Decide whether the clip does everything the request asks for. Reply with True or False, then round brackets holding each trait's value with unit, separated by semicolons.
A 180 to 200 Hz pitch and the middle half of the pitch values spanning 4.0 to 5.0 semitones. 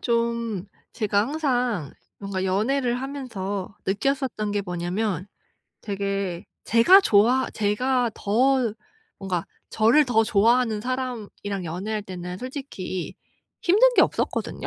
False (215 Hz; 4.3 semitones)